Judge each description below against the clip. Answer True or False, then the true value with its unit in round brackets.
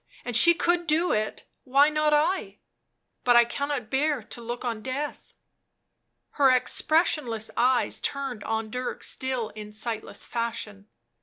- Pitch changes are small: False (4.7 semitones)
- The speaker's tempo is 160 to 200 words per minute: False (145 wpm)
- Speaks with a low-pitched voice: False (250 Hz)